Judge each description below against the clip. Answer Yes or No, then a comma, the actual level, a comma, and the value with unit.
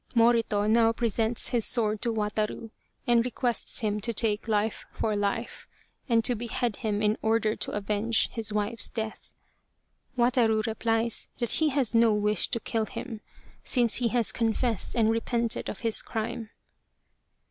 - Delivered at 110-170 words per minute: Yes, average, 160 wpm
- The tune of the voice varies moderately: No, narrow, 1.7 semitones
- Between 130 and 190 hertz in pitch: No, high, 225 Hz